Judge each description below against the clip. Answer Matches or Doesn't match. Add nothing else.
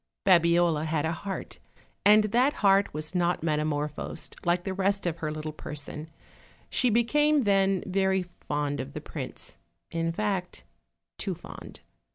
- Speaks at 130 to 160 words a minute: Matches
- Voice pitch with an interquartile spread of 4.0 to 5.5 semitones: Matches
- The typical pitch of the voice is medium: Matches